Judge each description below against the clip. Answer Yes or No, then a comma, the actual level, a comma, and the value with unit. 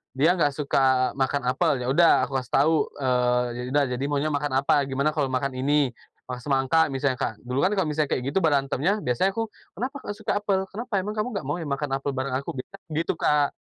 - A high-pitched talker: No, medium, 140 Hz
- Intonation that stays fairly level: No, average, 4.0 semitones